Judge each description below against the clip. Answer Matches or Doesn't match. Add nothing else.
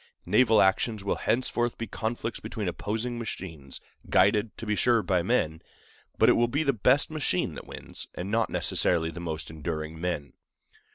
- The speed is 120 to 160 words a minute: Doesn't match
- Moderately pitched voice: Doesn't match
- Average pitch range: Doesn't match